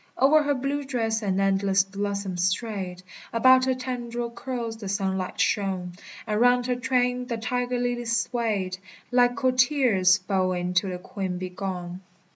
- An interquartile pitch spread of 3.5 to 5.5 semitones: Yes, average, 4.5 semitones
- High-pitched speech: Yes, high, 225 Hz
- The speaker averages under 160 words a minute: Yes, average, 150 wpm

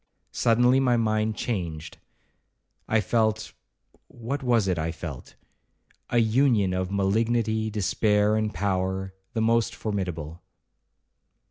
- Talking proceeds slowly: Yes, slow, 100 wpm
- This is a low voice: Yes, low, 110 Hz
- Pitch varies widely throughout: No, average, 3.4 semitones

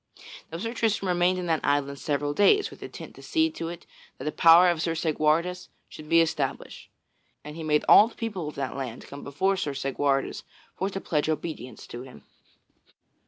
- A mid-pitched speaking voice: Yes, medium, 160 Hz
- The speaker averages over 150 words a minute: Yes, average, 195 wpm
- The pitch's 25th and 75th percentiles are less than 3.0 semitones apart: No, average, 4.1 semitones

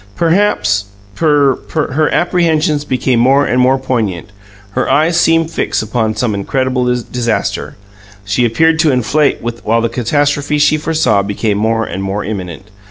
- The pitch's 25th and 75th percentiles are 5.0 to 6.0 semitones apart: Yes, wide, 5.6 semitones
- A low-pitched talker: Yes, low, 125 Hz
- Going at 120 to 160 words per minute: Yes, average, 155 wpm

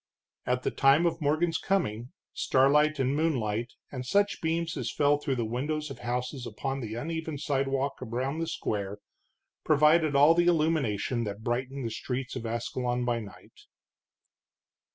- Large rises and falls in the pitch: No, average, 4.1 semitones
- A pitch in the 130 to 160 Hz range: Yes, low, 135 Hz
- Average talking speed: Yes, average, 155 wpm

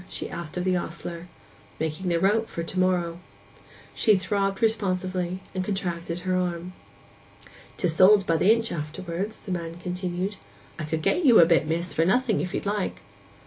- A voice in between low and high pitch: Yes, medium, 180 Hz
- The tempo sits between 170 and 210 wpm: Yes, average, 175 wpm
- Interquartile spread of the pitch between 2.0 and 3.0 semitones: Yes, narrow, 2.5 semitones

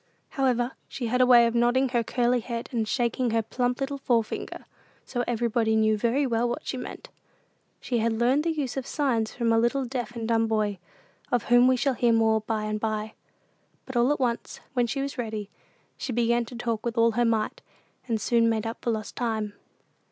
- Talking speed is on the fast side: Yes, fast, 210 wpm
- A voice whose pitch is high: Yes, high, 235 Hz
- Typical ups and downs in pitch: No, narrow, 1.9 semitones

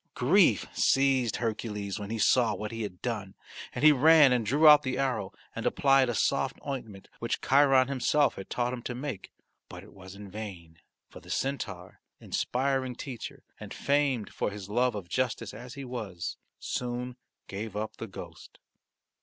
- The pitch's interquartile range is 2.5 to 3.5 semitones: No, average, 4.4 semitones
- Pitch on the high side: No, low, 120 Hz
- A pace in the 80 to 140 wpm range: No, average, 175 wpm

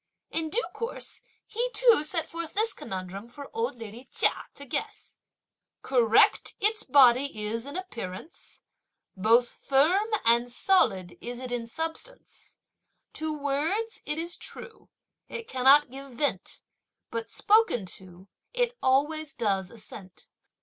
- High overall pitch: Yes, very high, 275 Hz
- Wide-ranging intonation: Yes, wide, 6.9 semitones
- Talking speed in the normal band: No, slow, 130 wpm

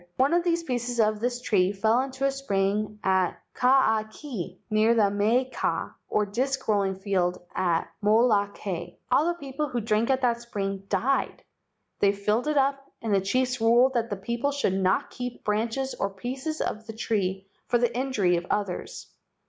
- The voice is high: Yes, high, 225 Hz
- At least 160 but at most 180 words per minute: Yes, average, 175 wpm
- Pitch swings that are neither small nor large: Yes, average, 4.5 semitones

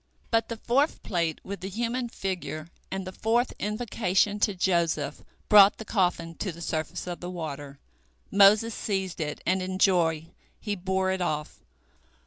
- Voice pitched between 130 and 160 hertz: No, high, 190 Hz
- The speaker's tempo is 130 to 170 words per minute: Yes, average, 160 wpm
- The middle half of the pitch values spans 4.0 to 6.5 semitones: No, average, 3.6 semitones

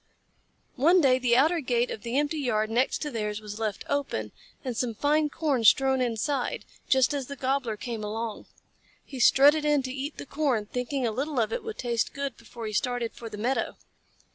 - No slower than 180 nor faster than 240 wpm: Yes, average, 200 wpm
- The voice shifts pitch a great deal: No, average, 3.8 semitones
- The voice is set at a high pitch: Yes, very high, 255 Hz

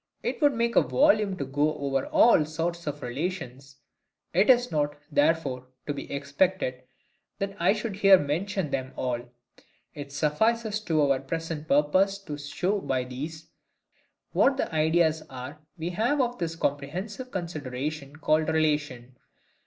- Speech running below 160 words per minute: Yes, average, 145 wpm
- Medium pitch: Yes, medium, 155 Hz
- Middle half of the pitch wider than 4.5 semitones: Yes, average, 5.2 semitones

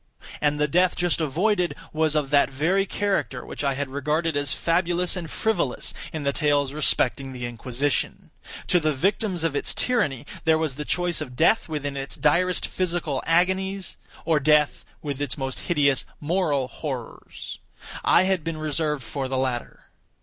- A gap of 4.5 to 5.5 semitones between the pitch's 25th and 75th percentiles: No, average, 4.1 semitones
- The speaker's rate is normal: Yes, average, 165 wpm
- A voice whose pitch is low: No, medium, 150 Hz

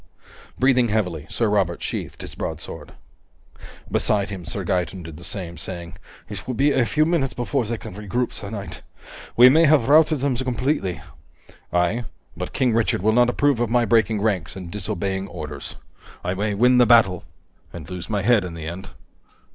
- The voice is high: No, low, 105 Hz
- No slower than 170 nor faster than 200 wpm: Yes, average, 180 wpm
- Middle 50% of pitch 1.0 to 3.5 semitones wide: No, average, 5.1 semitones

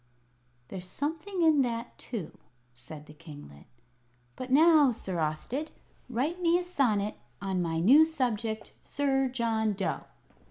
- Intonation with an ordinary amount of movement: No, wide, 8.1 semitones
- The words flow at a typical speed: No, slow, 130 wpm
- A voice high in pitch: Yes, high, 235 Hz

